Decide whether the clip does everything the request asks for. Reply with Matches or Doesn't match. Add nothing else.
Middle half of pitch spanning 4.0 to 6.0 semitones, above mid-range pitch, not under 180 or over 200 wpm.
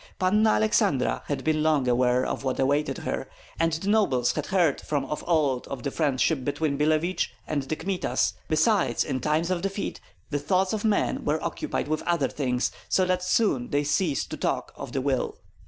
Doesn't match